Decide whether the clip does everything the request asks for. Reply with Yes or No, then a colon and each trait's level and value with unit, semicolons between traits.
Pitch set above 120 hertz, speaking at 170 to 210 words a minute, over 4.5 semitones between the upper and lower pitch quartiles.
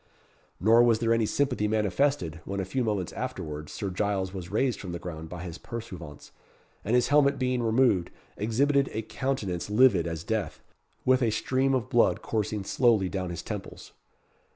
No: low, 110 Hz; average, 175 wpm; wide, 5.5 semitones